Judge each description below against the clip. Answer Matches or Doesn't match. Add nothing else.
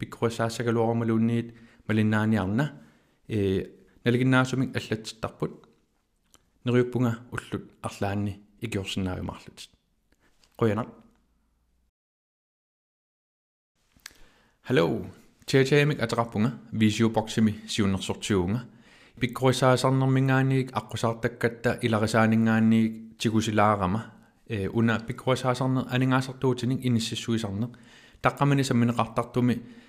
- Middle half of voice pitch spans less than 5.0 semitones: Matches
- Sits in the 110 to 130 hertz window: Matches